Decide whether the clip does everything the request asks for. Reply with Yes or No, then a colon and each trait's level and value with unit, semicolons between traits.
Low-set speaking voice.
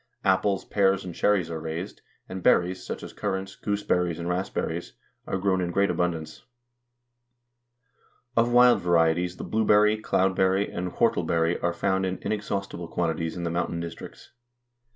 Yes: very low, 90 Hz